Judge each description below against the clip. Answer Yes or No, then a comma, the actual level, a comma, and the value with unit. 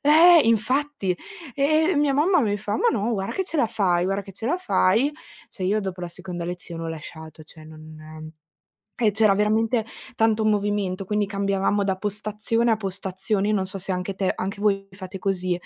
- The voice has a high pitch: Yes, high, 200 Hz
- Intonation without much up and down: No, average, 3.2 semitones